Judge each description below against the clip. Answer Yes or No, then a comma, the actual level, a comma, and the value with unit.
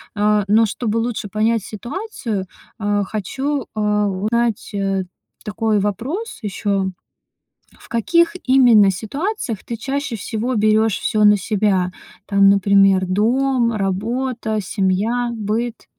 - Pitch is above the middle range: Yes, high, 215 Hz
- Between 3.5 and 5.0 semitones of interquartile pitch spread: No, average, 3.0 semitones